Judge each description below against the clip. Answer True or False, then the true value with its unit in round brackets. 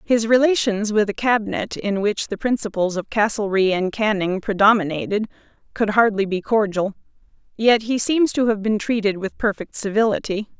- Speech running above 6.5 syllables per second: False (5.1 syllables/s)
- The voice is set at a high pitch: True (210 Hz)